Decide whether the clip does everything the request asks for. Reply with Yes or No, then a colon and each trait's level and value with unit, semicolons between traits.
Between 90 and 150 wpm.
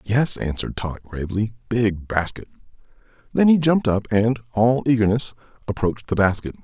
Yes: average, 145 wpm